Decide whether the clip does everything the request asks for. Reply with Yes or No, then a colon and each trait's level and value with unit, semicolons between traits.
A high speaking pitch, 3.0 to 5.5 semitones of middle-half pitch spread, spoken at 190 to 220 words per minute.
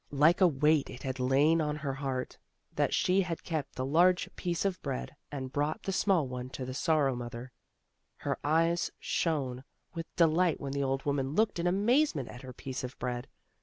No: medium, 145 Hz; average, 4.4 semitones; average, 195 wpm